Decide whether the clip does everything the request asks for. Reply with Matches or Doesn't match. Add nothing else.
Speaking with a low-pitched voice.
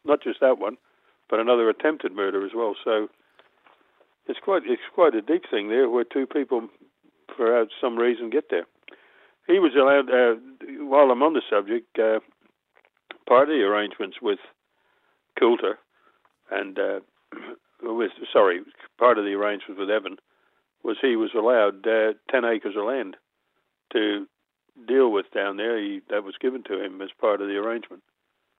Doesn't match